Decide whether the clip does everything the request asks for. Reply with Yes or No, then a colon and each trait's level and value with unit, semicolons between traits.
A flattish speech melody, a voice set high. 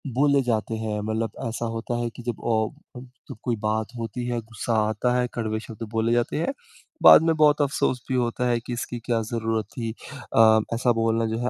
No: narrow, 1.8 semitones; low, 115 Hz